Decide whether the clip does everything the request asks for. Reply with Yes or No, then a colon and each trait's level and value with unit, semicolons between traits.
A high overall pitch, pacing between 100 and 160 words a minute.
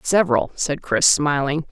No: medium, 155 Hz; average, 140 wpm